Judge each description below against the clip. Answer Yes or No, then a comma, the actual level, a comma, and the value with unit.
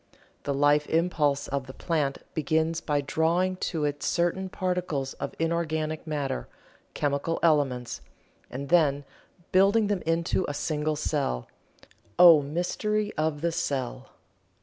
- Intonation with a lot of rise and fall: No, average, 3.0 semitones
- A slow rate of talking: Yes, slow, 125 wpm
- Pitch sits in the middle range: Yes, medium, 155 Hz